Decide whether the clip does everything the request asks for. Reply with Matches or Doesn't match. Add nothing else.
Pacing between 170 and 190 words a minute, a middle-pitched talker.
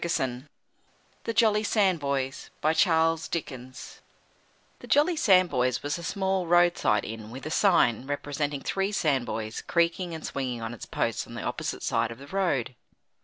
Doesn't match